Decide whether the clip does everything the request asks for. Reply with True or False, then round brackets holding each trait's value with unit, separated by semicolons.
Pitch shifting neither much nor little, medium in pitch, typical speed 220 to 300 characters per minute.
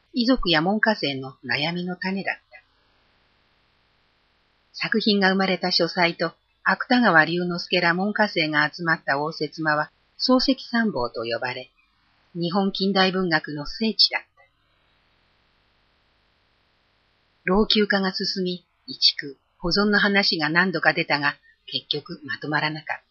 True (4.6 semitones; 175 Hz; 235 characters per minute)